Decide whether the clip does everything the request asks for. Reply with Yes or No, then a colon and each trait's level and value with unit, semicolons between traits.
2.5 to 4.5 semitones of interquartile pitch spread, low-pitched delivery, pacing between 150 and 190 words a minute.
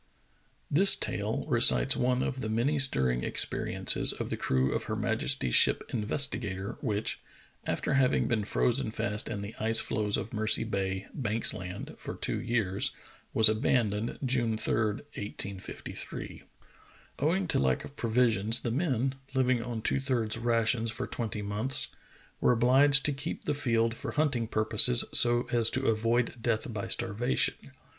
Yes: average, 3.2 semitones; low, 115 Hz; average, 155 wpm